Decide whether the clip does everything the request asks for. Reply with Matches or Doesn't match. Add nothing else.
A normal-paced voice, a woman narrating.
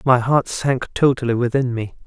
Doesn't match